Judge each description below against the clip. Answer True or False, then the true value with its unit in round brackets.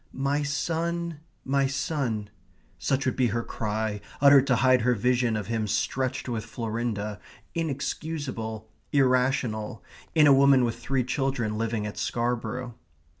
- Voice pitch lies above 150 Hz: False (125 Hz)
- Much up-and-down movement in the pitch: False (3.7 semitones)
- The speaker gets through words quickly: False (135 wpm)